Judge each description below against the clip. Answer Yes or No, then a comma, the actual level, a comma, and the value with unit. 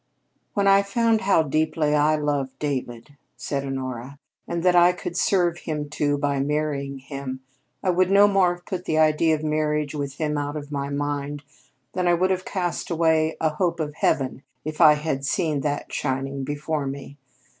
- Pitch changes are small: No, average, 3.4 semitones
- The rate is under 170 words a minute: No, average, 185 wpm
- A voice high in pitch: No, medium, 150 Hz